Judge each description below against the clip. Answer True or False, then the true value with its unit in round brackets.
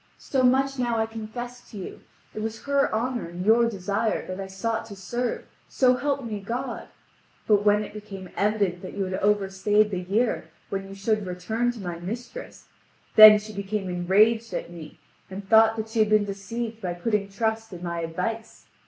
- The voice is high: True (215 Hz)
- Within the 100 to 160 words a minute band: False (190 wpm)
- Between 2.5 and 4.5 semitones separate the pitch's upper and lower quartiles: True (3.0 semitones)